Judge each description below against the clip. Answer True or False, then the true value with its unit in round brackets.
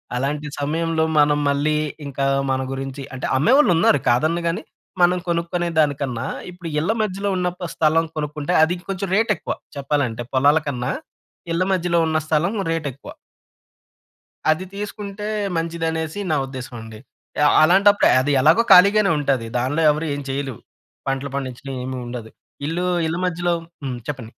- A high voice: False (155 Hz)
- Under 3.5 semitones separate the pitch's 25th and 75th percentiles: False (4.3 semitones)